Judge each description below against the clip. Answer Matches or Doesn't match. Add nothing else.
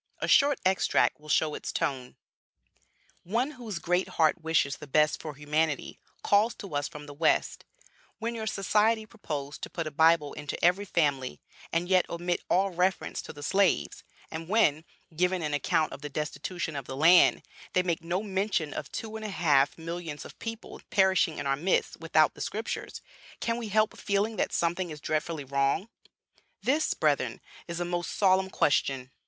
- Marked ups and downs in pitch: Doesn't match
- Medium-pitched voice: Matches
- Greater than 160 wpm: Matches